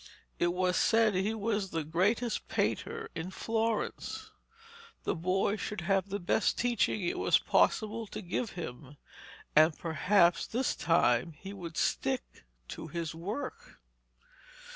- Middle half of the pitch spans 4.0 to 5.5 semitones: Yes, average, 4.5 semitones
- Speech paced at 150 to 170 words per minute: No, slow, 135 wpm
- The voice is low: No, medium, 185 Hz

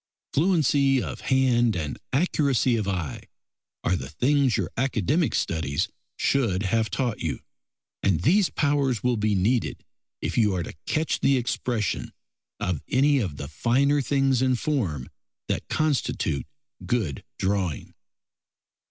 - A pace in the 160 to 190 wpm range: No, slow, 135 wpm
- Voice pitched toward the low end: Yes, low, 120 Hz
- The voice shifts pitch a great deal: Yes, wide, 6.4 semitones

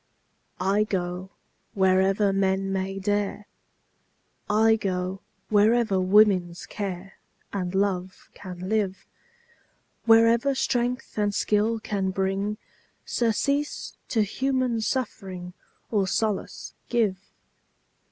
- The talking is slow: Yes, slow, 95 wpm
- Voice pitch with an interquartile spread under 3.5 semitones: Yes, average, 2.7 semitones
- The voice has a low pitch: No, high, 200 Hz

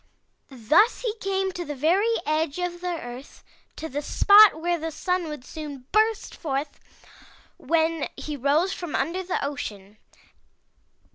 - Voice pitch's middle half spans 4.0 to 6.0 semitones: Yes, average, 4.4 semitones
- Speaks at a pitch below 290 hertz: No, very high, 320 Hz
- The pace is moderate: Yes, average, 145 wpm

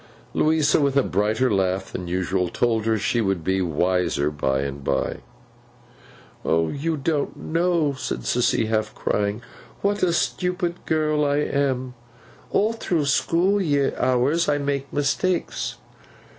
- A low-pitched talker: Yes, low, 130 Hz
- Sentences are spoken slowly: Yes, slow, 130 wpm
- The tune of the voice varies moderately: No, wide, 8.2 semitones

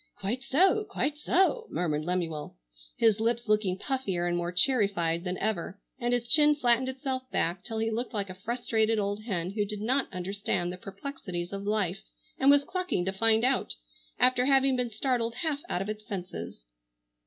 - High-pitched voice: Yes, high, 215 Hz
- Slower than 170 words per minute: No, average, 185 wpm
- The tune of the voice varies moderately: No, wide, 5.7 semitones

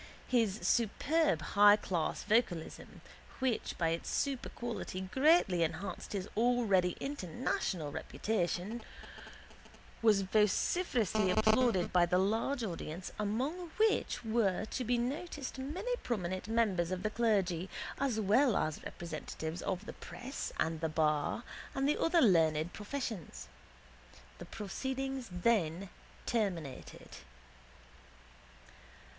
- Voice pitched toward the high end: Yes, high, 210 Hz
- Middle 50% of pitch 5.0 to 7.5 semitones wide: Yes, wide, 5.6 semitones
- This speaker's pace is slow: Yes, slow, 105 wpm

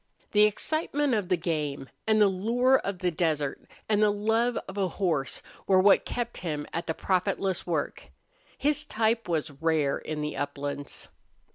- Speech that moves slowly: No, average, 165 wpm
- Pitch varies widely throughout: Yes, wide, 5.8 semitones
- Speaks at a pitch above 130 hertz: Yes, medium, 185 Hz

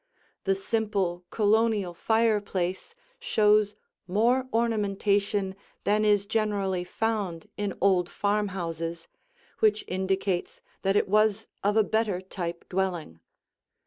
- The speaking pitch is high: Yes, high, 200 Hz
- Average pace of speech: No, slow, 105 wpm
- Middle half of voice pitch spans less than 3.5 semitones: Yes, narrow, 2.4 semitones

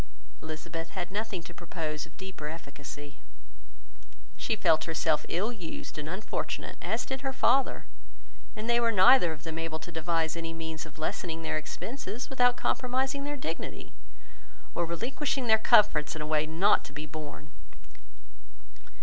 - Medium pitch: Yes, medium, 170 Hz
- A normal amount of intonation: No, wide, 5.9 semitones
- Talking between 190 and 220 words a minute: No, average, 155 wpm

